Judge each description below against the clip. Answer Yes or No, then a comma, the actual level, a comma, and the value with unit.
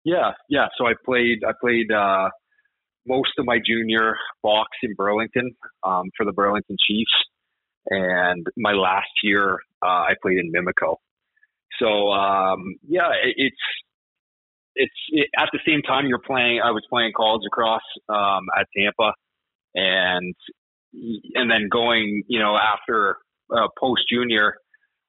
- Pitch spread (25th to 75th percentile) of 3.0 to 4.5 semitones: Yes, average, 3.7 semitones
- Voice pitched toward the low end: Yes, low, 110 Hz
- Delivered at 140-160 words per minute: Yes, average, 145 wpm